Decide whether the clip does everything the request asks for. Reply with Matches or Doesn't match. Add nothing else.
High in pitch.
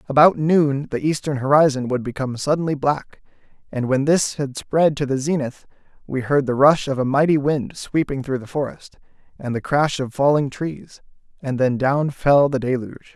Doesn't match